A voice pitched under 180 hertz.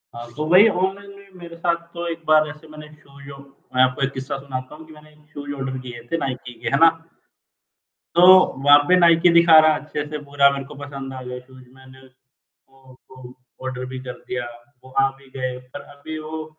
Yes: medium, 140 Hz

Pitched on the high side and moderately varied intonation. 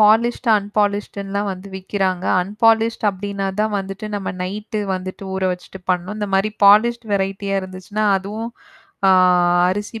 No: high, 200 Hz; narrow, 1.9 semitones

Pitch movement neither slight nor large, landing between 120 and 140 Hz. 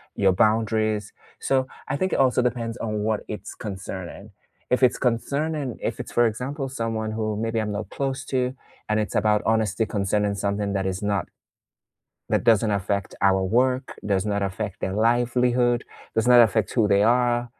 No: average, 3.1 semitones; low, 110 Hz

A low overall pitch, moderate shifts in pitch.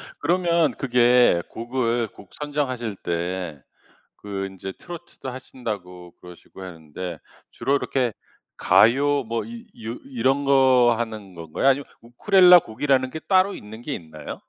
No: low, 120 Hz; wide, 6.7 semitones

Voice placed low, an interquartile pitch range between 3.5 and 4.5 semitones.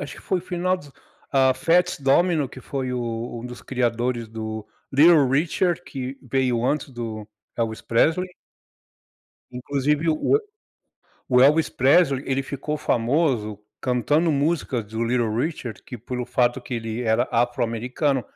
Yes: low, 130 Hz; average, 4.0 semitones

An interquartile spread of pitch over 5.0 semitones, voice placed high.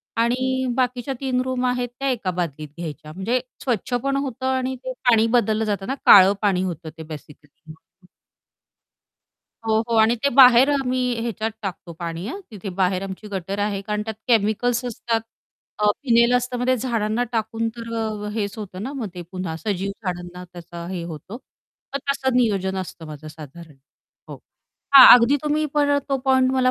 Yes: wide, 5.4 semitones; high, 220 Hz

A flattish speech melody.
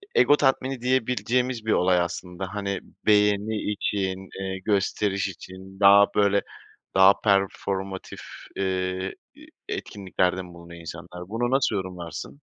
Yes: narrow, 2.1 semitones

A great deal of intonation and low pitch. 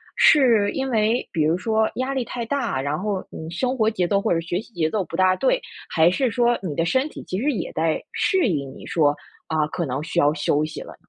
No: wide, 7.1 semitones; high, 190 Hz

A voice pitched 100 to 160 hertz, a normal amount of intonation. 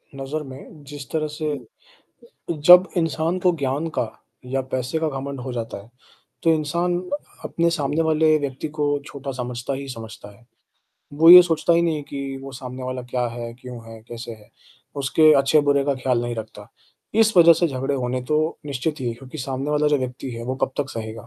Yes: low, 135 Hz; average, 3.7 semitones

